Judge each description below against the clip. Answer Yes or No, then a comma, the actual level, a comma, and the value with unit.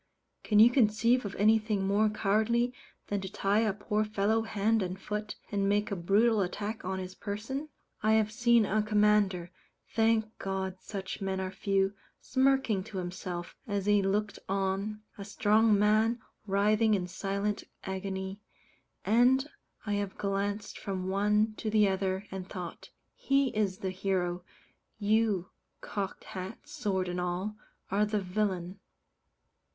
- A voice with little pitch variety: Yes, narrow, 2.0 semitones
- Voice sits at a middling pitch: No, high, 205 Hz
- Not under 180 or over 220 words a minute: No, average, 150 wpm